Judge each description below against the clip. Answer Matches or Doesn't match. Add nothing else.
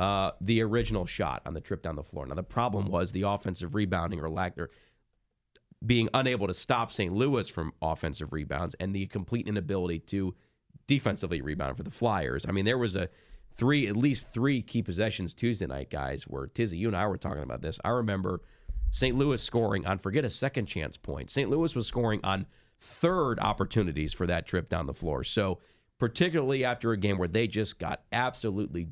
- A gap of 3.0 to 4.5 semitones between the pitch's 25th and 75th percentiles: Doesn't match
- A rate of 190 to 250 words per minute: Matches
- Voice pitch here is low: Matches